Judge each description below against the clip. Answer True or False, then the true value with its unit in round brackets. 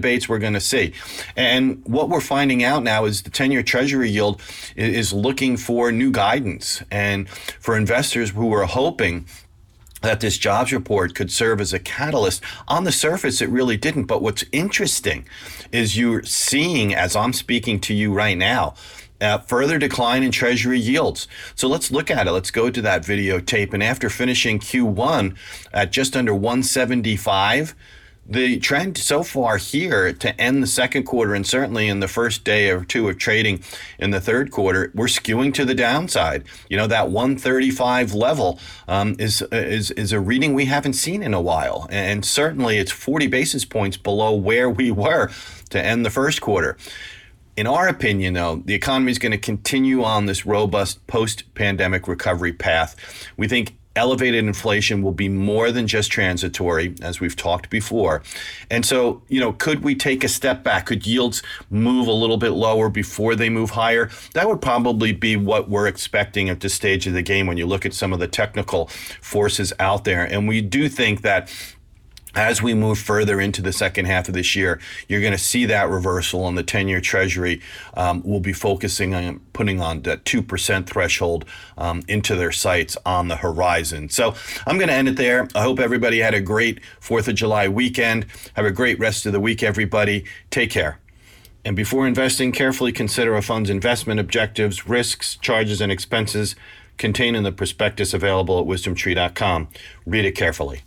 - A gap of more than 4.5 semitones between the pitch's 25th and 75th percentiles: False (3.9 semitones)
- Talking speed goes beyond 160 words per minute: True (185 wpm)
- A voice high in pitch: False (105 Hz)